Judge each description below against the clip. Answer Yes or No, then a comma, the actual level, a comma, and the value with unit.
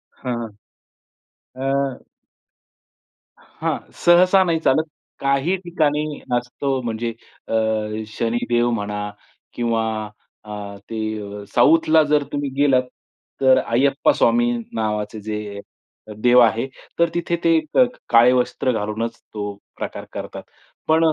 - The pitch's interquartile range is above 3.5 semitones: Yes, average, 4.8 semitones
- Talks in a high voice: No, low, 125 Hz